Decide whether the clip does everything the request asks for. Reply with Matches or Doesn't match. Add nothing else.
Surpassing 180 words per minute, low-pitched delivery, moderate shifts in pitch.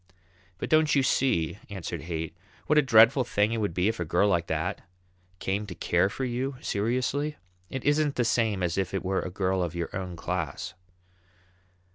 Doesn't match